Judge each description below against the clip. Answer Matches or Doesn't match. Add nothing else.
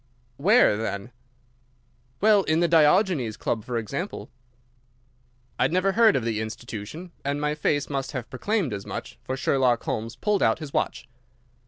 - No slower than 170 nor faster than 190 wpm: Doesn't match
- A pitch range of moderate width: Doesn't match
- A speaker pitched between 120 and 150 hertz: Matches